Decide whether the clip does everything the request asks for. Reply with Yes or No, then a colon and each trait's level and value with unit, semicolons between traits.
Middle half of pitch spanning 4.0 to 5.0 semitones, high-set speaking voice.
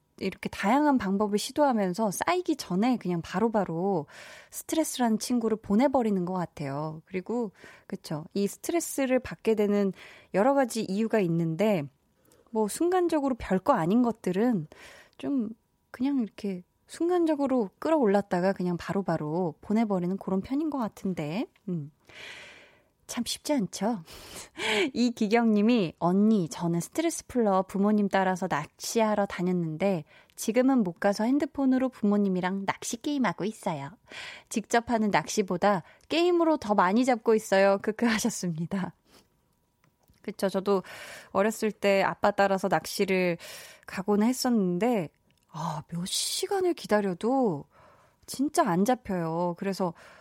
Yes: average, 4.7 semitones; high, 205 Hz